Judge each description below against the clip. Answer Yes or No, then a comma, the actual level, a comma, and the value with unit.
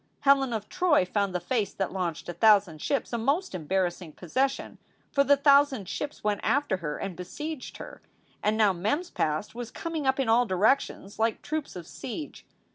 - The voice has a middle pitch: No, high, 220 Hz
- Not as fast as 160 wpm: No, average, 190 wpm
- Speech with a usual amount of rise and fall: No, wide, 7.1 semitones